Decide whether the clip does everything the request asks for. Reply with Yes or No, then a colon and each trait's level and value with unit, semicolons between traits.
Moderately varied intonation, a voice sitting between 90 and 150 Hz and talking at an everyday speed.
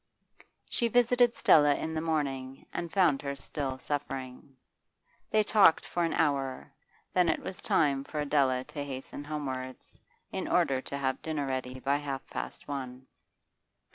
Yes: average, 3.2 semitones; medium, 140 Hz; average, 150 wpm